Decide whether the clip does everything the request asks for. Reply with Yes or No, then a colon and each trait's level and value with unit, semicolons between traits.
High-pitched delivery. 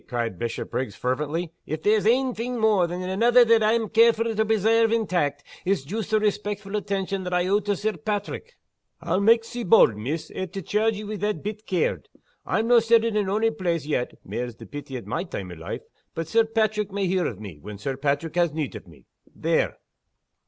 Yes: high, 200 Hz